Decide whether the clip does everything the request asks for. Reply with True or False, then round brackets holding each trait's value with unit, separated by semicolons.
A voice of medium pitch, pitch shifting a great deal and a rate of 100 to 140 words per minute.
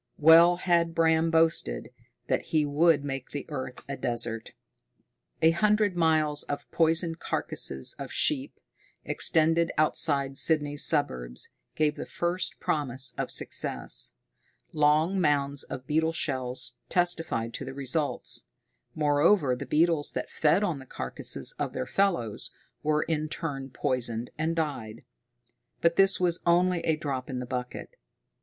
False (150 Hz; 3.8 semitones; 135 wpm)